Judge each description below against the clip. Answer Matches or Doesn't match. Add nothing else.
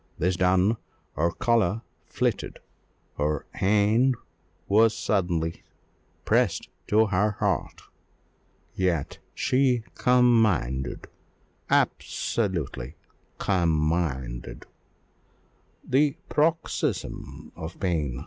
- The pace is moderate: Doesn't match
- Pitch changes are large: Matches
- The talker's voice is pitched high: Doesn't match